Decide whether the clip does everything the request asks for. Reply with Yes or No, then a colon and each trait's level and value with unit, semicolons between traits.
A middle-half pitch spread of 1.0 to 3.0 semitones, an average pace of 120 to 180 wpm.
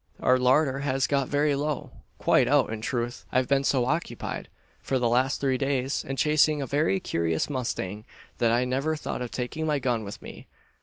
No: average, 2.7 semitones; average, 195 wpm